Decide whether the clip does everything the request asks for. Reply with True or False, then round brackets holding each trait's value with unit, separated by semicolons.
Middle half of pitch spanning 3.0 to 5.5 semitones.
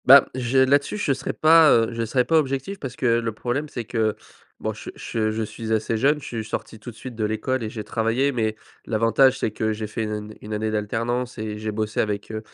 True (3.3 semitones)